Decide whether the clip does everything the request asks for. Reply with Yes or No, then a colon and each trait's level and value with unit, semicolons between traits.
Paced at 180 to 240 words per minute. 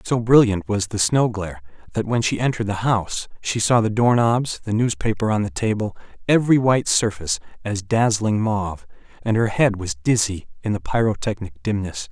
Yes: average, 185 wpm